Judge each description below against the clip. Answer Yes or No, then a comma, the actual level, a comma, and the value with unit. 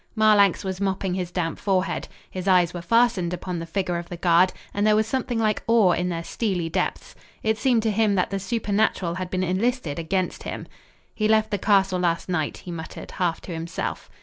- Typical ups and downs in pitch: Yes, average, 3.5 semitones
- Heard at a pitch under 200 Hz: Yes, high, 190 Hz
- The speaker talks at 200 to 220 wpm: Yes, fast, 205 wpm